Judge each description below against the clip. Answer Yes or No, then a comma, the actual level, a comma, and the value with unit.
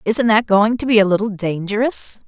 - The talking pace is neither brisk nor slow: No, fast, 210 wpm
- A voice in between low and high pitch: No, high, 210 Hz